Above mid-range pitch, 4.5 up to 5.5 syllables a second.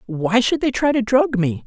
Yes: high, 215 Hz; 4.6 syllables/s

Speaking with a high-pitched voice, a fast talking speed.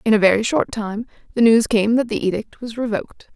Yes: high, 225 Hz; fast, 230 wpm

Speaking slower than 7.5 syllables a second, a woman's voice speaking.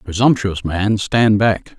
No: 3.6 syllables/s; male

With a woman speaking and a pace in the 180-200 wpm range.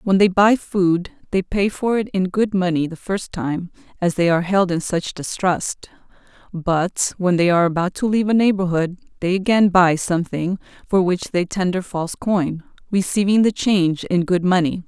Yes: female; average, 185 wpm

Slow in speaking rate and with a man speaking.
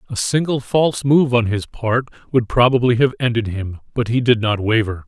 No: average, 200 wpm; male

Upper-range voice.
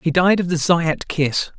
No: medium, 165 Hz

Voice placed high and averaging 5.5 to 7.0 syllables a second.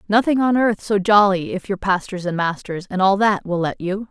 No: high, 195 Hz; 5.1 syllables/s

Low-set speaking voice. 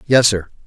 Yes: low, 110 Hz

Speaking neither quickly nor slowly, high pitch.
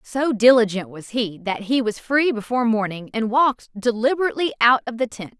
Yes: average, 190 wpm; high, 235 Hz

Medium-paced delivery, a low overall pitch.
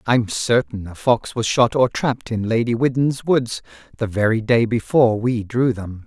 Yes: average, 190 wpm; low, 115 Hz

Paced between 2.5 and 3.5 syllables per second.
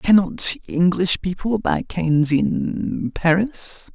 Yes: 3.2 syllables/s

